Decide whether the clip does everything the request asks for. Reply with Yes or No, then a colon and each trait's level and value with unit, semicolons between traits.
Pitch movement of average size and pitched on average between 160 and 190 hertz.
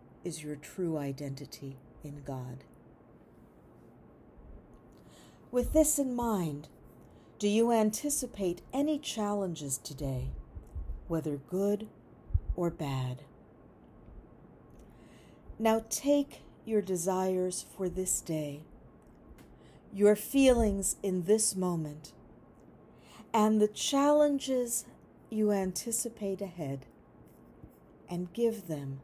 No: wide, 7.5 semitones; medium, 185 Hz